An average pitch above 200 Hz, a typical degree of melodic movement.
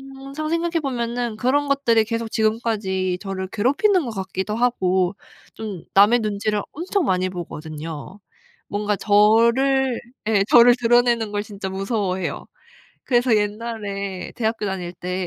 Yes: high, 215 Hz; average, 4.0 semitones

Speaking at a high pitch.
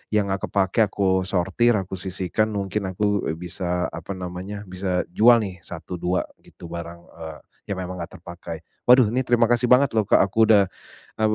No: very low, 95 Hz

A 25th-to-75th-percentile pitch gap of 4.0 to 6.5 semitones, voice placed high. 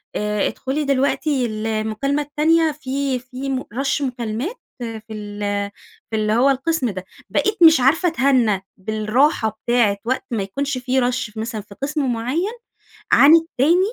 Yes: average, 4.8 semitones; very high, 255 Hz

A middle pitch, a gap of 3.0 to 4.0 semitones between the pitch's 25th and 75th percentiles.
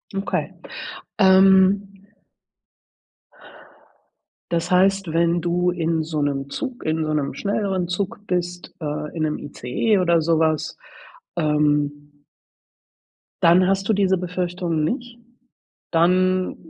Yes: medium, 175 Hz; average, 3.4 semitones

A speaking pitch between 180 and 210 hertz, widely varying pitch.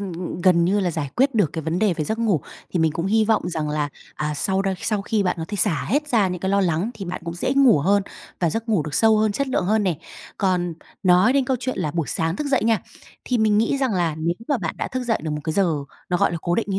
No: high, 190 Hz; average, 4.7 semitones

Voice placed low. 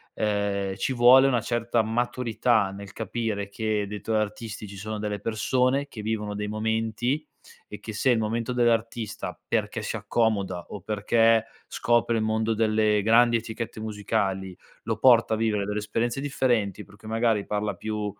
Yes: low, 110 Hz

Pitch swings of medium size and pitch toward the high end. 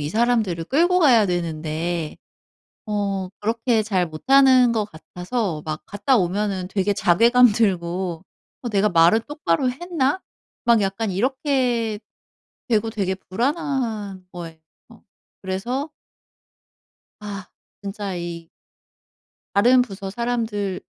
Yes: average, 4.9 semitones; high, 205 Hz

